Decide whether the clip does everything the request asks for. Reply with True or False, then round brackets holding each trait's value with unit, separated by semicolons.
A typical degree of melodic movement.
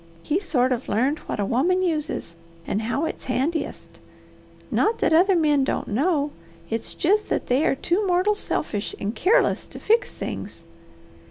False (6.6 semitones)